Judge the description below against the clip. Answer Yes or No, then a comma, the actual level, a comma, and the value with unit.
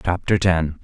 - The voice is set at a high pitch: No, very low, 85 Hz